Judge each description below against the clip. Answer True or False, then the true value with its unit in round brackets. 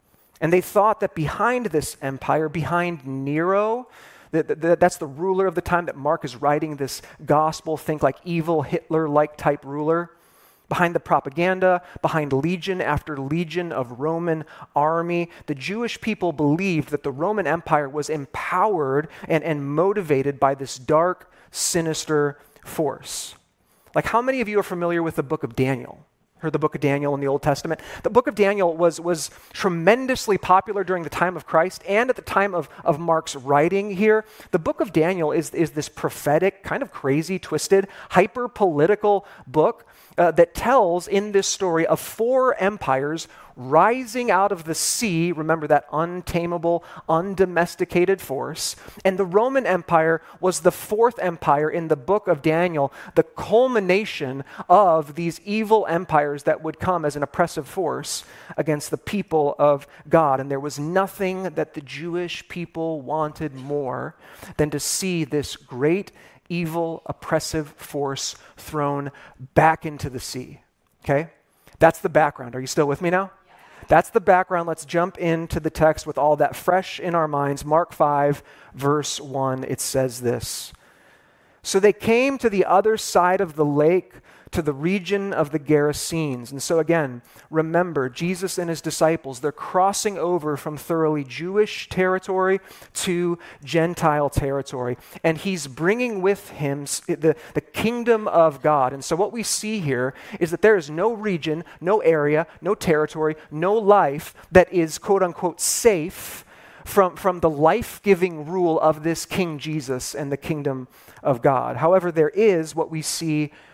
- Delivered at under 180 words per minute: True (160 wpm)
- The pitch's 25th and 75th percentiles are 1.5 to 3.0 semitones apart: False (3.8 semitones)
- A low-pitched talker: False (165 Hz)